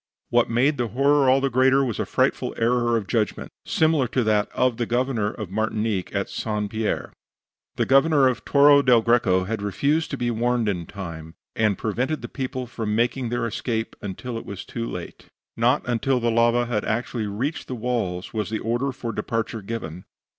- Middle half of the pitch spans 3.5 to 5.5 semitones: No, average, 3.0 semitones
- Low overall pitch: Yes, low, 115 Hz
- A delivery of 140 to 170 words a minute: No, average, 190 wpm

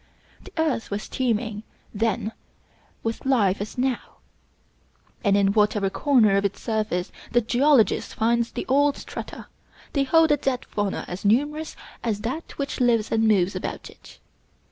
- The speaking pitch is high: Yes, high, 225 Hz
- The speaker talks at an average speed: Yes, average, 150 wpm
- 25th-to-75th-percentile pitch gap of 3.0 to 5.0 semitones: Yes, average, 4.4 semitones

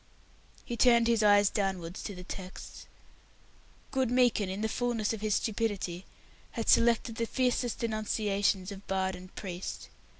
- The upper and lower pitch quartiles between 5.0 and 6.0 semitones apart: No, average, 3.3 semitones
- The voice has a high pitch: Yes, high, 210 Hz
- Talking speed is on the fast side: No, average, 145 wpm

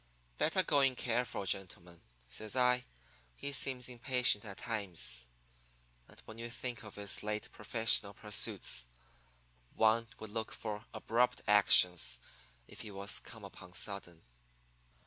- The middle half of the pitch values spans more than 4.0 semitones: No, average, 3.5 semitones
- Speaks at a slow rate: Yes, slow, 130 wpm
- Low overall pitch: Yes, low, 110 Hz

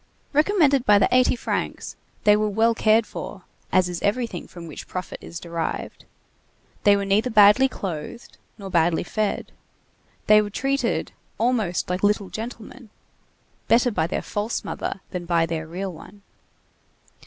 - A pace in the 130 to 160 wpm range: Yes, average, 145 wpm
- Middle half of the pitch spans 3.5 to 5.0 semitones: Yes, average, 4.4 semitones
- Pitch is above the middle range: Yes, high, 205 Hz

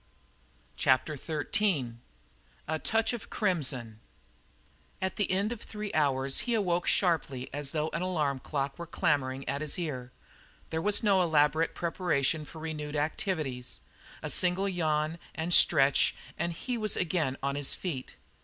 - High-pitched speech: No, medium, 160 Hz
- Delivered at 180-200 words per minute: No, average, 145 wpm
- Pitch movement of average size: Yes, average, 4.6 semitones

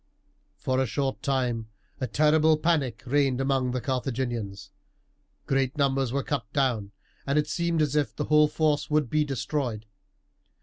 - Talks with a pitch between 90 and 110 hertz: No, low, 135 Hz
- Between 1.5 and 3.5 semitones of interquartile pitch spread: Yes, average, 3.1 semitones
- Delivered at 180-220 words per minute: No, average, 155 wpm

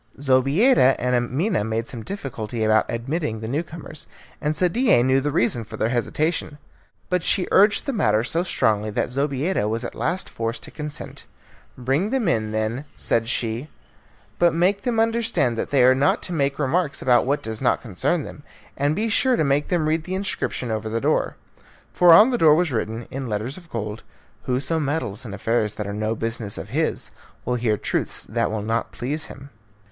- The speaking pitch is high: No, low, 135 Hz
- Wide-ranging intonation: Yes, wide, 6.5 semitones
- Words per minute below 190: No, average, 195 wpm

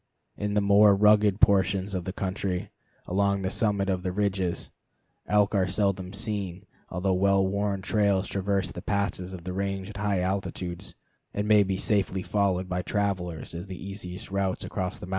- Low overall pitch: Yes, very low, 95 Hz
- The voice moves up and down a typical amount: No, narrow, 1.6 semitones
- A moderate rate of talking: Yes, average, 180 wpm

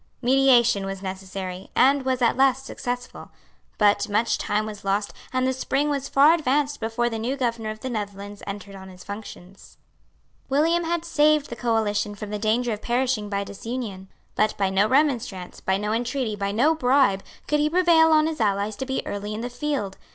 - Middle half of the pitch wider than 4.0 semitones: Yes, average, 4.9 semitones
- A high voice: Yes, high, 230 Hz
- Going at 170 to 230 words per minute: Yes, average, 190 wpm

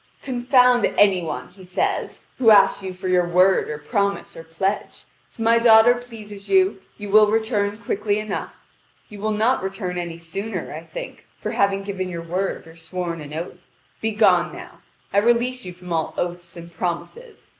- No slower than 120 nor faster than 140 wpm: No, average, 175 wpm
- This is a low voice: No, high, 200 Hz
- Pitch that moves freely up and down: No, average, 3.8 semitones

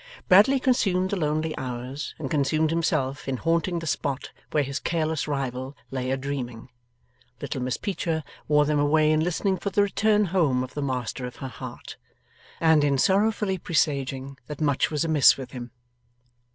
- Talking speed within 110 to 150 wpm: No, average, 170 wpm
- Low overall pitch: No, medium, 150 Hz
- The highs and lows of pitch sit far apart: No, average, 3.9 semitones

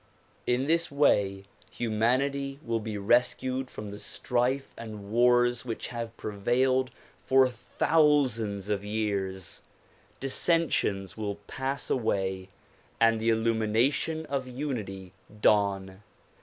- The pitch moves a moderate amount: Yes, average, 4.2 semitones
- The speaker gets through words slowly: Yes, slow, 105 wpm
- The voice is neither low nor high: No, low, 115 Hz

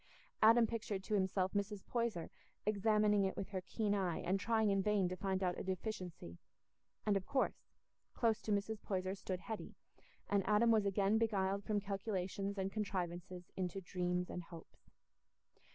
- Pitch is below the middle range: No, high, 195 Hz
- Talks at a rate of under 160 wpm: No, average, 165 wpm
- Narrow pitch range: Yes, narrow, 2.3 semitones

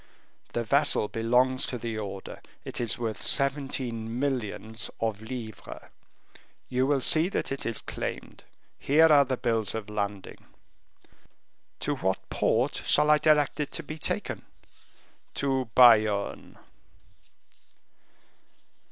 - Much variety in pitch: No, average, 4.0 semitones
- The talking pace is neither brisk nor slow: No, slow, 120 wpm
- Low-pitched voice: Yes, low, 125 Hz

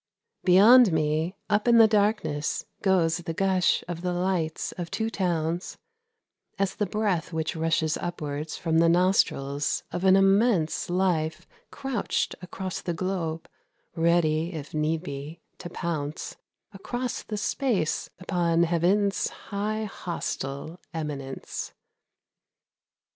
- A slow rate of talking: Yes, slow, 115 wpm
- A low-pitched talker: No, medium, 175 Hz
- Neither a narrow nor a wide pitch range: Yes, average, 3.4 semitones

